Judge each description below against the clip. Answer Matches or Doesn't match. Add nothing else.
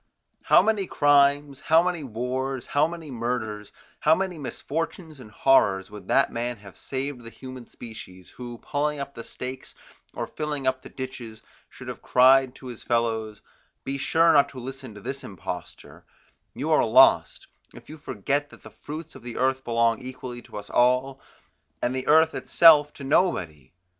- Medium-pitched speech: Doesn't match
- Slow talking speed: Doesn't match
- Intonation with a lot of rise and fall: Doesn't match